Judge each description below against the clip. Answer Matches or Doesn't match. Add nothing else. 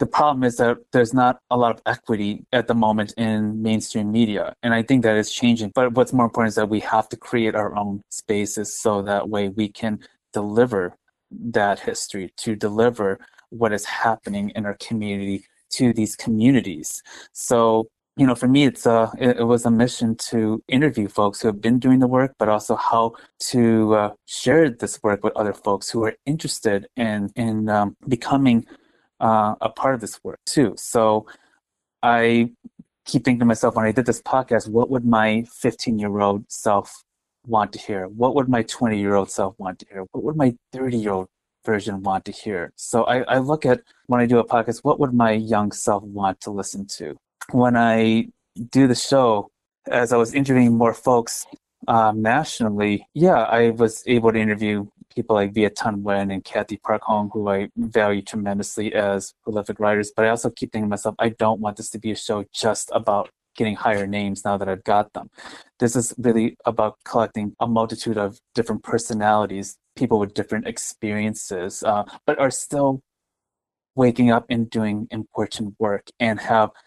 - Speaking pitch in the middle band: Doesn't match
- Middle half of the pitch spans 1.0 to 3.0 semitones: Matches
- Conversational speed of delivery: Matches